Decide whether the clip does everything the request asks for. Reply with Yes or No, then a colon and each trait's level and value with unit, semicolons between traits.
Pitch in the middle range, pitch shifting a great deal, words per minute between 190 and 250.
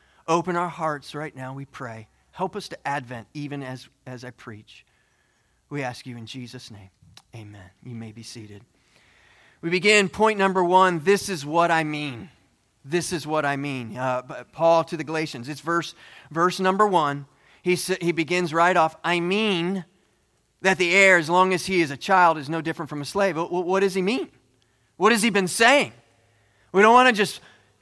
Yes: medium, 160 Hz; wide, 6.2 semitones; average, 195 wpm